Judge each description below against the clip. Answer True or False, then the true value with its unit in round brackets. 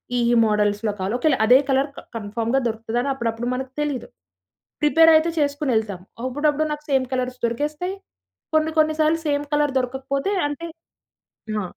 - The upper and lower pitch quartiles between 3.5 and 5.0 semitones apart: True (4.3 semitones)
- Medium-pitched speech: False (270 Hz)